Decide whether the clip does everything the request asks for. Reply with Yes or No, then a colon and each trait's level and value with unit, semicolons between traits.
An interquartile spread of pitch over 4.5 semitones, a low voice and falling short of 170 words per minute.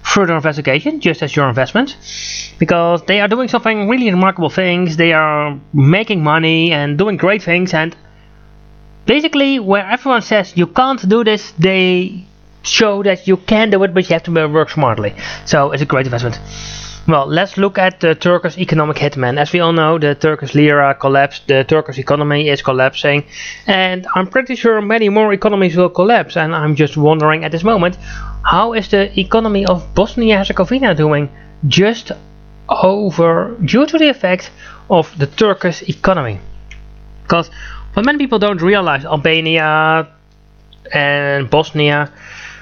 No: average, 5.2 semitones; medium, 170 Hz; average, 160 wpm